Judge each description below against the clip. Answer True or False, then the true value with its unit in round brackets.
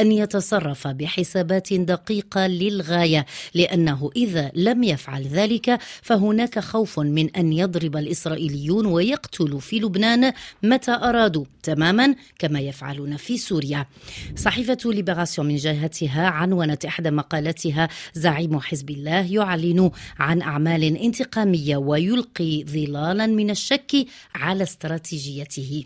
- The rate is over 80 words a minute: True (105 wpm)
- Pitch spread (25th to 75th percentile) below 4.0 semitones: False (5.5 semitones)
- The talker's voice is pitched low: False (175 Hz)